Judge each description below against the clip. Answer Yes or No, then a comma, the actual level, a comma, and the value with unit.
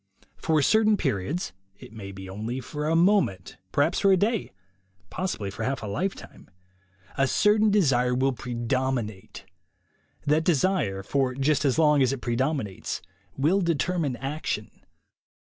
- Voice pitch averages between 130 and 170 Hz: Yes, low, 135 Hz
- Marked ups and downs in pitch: Yes, wide, 6.7 semitones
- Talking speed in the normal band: Yes, average, 145 wpm